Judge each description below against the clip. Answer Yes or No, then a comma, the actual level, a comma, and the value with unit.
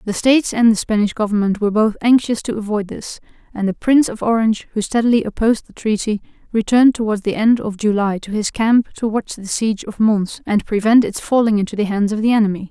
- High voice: Yes, high, 215 Hz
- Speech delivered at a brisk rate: Yes, fast, 220 wpm